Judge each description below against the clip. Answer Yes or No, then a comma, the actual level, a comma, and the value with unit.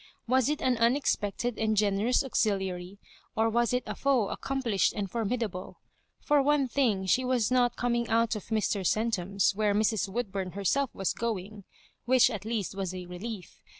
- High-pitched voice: Yes, high, 220 Hz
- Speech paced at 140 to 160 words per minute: No, average, 170 wpm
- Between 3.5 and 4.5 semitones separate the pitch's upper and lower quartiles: Yes, average, 3.8 semitones